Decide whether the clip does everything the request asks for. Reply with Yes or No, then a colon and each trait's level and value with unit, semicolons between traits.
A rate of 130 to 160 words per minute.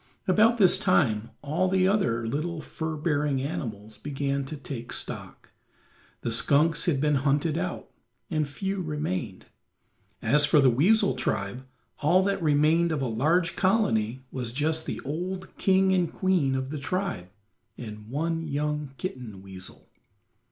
Yes: average, 145 wpm